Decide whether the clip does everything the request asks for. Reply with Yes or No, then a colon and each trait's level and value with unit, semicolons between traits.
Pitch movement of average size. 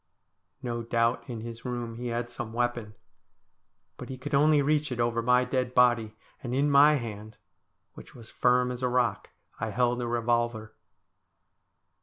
No: narrow, 1.4 semitones